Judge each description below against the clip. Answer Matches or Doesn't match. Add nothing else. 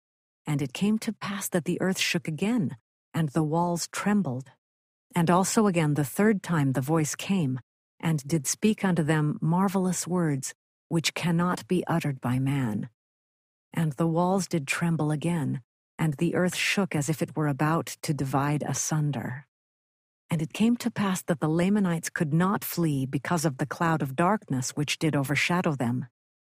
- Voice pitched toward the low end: Doesn't match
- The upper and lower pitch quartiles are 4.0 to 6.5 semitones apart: Doesn't match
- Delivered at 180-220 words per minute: Doesn't match